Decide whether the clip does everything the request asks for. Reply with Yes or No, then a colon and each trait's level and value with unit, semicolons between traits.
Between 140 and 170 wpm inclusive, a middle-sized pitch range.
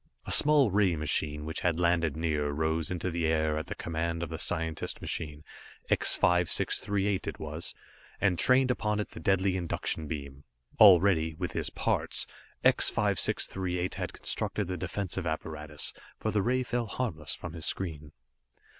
Yes: average, 160 wpm; average, 3.6 semitones